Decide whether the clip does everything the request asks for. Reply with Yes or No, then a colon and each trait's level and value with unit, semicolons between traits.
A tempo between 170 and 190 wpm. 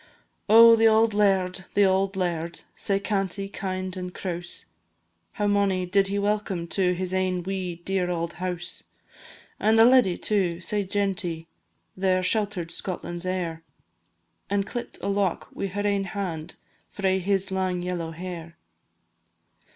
No: average, 145 wpm